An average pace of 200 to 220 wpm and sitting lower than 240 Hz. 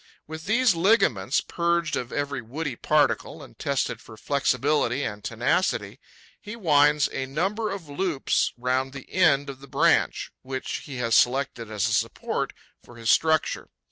No: average, 155 wpm; medium, 140 Hz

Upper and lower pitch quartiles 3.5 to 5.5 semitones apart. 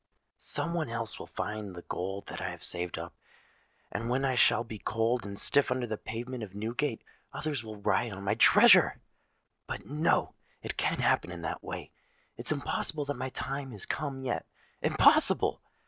Yes: average, 4.7 semitones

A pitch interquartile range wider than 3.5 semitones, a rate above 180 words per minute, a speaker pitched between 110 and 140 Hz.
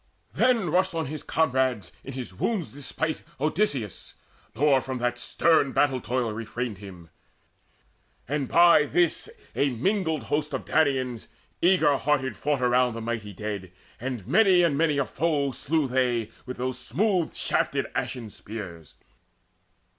No: average, 4.8 semitones; average, 140 wpm; low, 135 Hz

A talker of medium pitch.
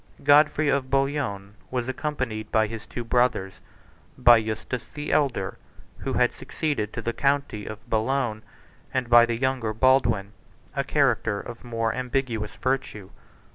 No: low, 120 Hz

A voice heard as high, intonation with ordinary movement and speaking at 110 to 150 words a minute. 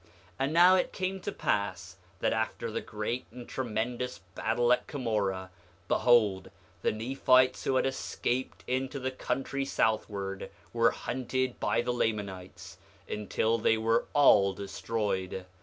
No: low, 115 Hz; average, 4.2 semitones; average, 140 wpm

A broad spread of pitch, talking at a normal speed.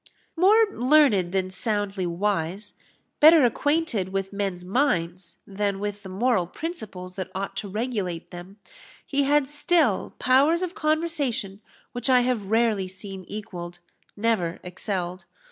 No: wide, 5.9 semitones; slow, 130 wpm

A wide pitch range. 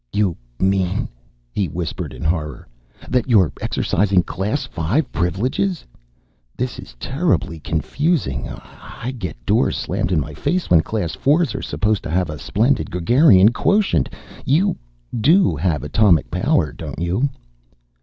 Yes: wide, 7.9 semitones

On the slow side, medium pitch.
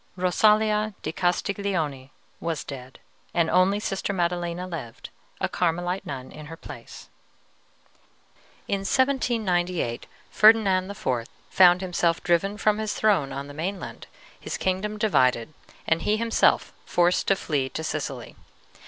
Yes: slow, 125 wpm; medium, 180 Hz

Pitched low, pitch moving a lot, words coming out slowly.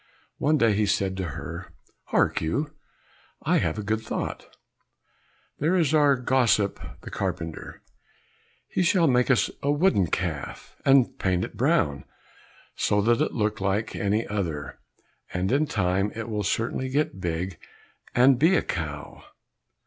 No: low, 105 Hz; wide, 6.3 semitones; average, 150 wpm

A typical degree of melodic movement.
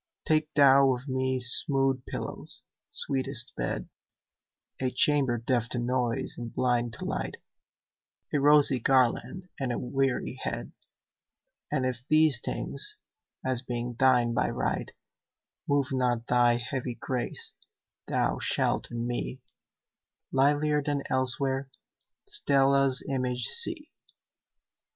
No: narrow, 2.2 semitones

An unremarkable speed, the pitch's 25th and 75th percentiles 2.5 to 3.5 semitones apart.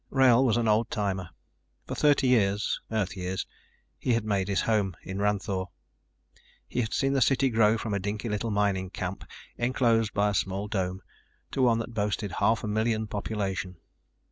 Yes: average, 175 wpm; average, 2.8 semitones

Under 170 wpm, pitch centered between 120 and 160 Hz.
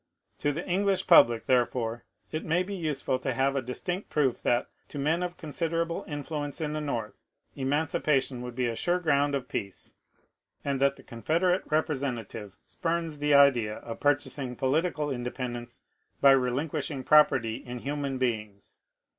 Yes: average, 160 wpm; medium, 140 Hz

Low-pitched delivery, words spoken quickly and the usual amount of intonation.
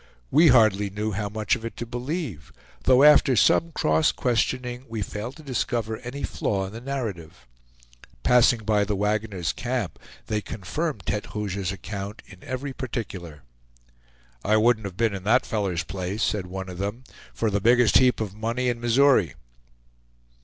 No: low, 110 Hz; average, 165 wpm; average, 3.9 semitones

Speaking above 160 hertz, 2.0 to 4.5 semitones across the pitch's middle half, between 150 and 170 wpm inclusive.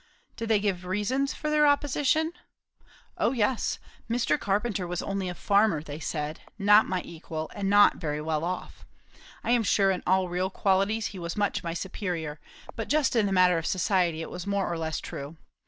No: high, 190 Hz; average, 4.1 semitones; average, 195 wpm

